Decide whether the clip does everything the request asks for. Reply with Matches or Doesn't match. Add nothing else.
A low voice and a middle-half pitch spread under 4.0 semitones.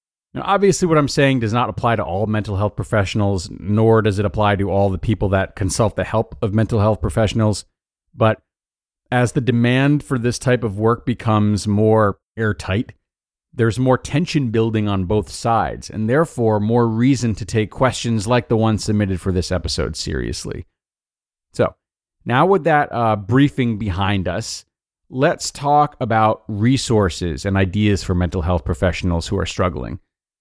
Matches